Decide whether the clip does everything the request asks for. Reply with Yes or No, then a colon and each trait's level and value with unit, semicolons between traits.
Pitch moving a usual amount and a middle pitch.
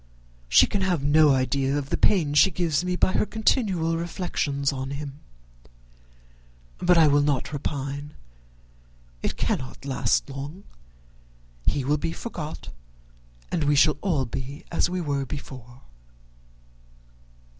Yes: average, 3.6 semitones; medium, 145 Hz